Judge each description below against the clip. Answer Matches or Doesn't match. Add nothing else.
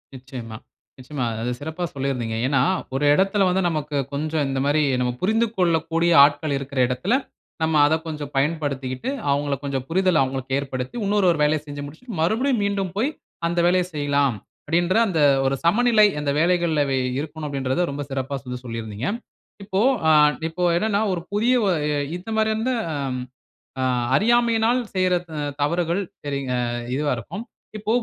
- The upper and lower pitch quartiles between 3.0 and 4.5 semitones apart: Doesn't match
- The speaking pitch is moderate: Matches